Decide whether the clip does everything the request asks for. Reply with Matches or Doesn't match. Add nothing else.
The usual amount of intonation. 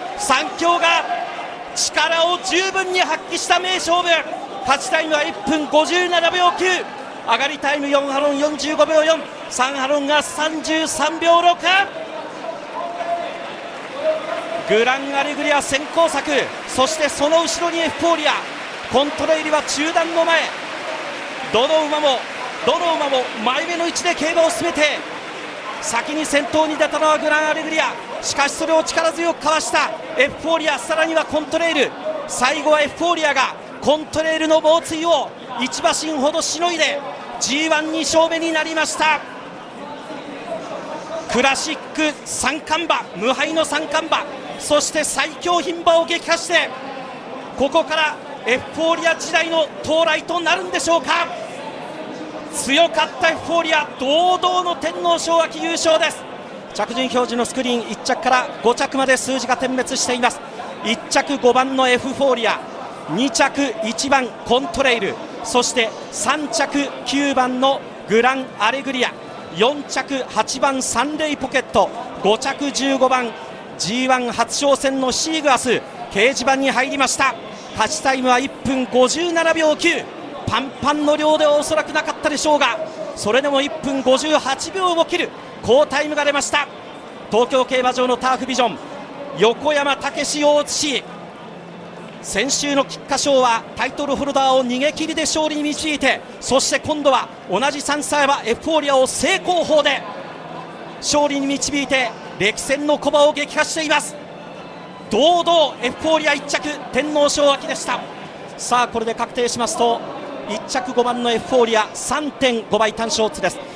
Matches